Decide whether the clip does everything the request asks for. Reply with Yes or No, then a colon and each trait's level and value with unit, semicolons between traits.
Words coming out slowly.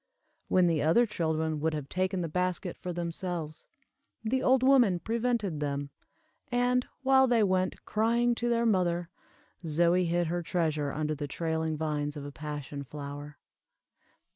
No: average, 150 wpm